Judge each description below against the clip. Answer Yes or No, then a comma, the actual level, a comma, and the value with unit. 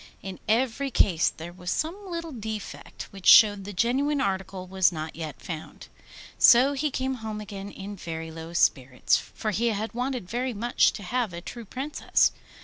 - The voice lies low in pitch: No, high, 210 Hz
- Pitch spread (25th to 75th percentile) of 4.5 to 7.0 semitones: Yes, wide, 5.6 semitones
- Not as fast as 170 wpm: No, average, 175 wpm